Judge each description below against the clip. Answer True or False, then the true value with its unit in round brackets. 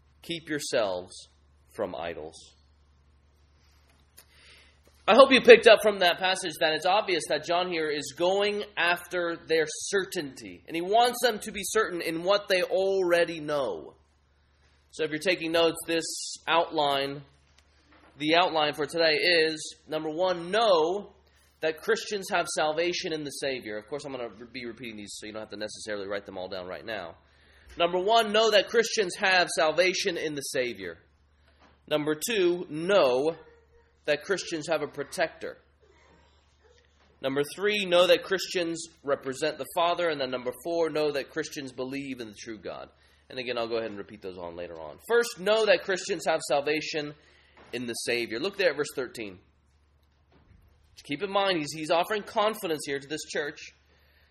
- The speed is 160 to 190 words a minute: True (165 wpm)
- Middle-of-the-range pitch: True (150 Hz)